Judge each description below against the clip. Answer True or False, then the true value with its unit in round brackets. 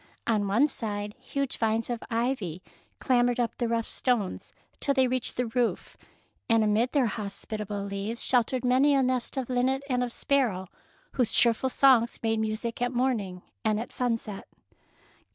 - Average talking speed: True (170 wpm)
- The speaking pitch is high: True (235 Hz)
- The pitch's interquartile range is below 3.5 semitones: True (2.8 semitones)